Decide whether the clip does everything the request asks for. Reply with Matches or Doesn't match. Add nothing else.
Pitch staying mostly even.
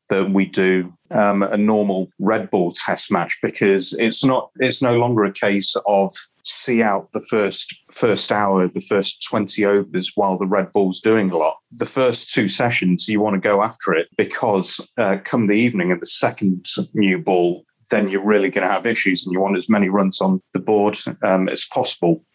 Matches